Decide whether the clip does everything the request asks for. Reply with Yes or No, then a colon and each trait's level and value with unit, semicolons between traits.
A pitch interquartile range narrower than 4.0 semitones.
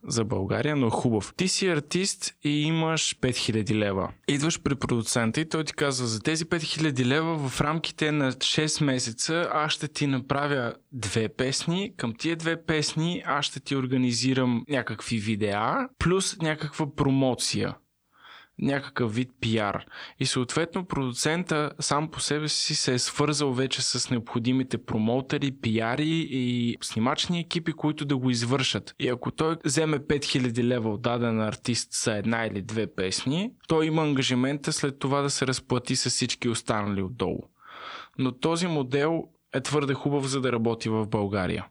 No: average, 4.3 semitones